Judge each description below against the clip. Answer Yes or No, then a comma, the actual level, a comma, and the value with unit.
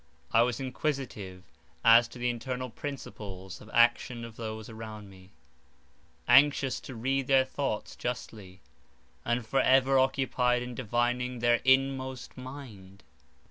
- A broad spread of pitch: No, average, 3.0 semitones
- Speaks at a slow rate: Yes, slow, 130 wpm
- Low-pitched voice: Yes, low, 120 Hz